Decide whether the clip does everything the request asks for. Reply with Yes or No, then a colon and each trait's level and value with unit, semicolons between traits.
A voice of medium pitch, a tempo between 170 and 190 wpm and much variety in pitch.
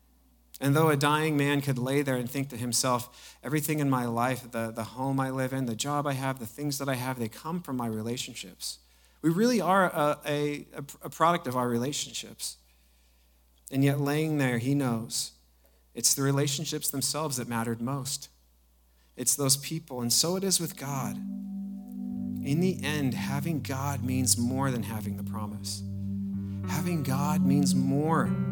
No: low, 130 Hz; average, 175 wpm; wide, 6.1 semitones